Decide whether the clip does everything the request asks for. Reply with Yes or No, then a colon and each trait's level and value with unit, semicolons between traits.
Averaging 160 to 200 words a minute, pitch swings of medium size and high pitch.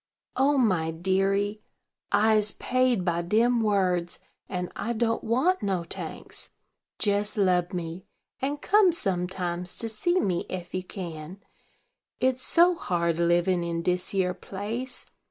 No: slow, 135 wpm; average, 4.7 semitones; high, 195 Hz